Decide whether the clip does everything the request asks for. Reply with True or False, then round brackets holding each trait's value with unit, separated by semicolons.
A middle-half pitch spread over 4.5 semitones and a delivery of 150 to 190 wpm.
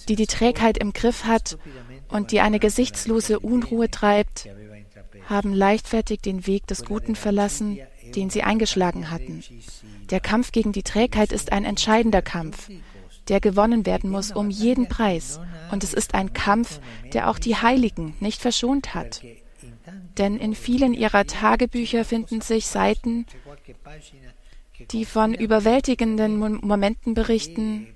False (5.0 semitones; 140 wpm)